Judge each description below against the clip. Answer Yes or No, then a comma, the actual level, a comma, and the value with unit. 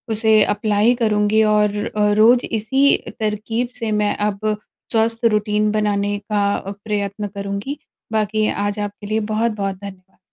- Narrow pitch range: Yes, narrow, 1.3 semitones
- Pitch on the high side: Yes, high, 210 Hz